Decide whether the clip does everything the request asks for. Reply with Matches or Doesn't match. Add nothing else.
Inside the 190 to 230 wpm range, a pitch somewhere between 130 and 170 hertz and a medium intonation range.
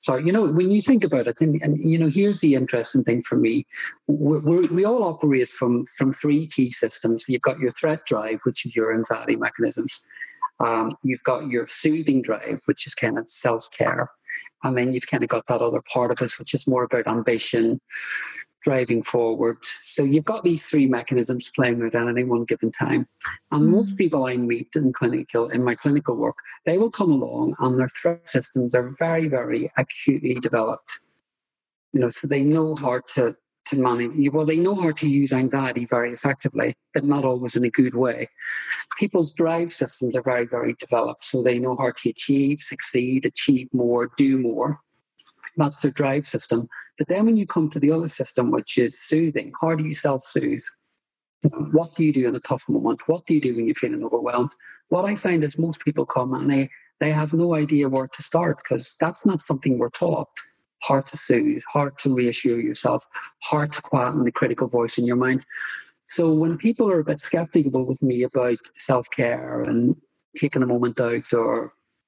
Matches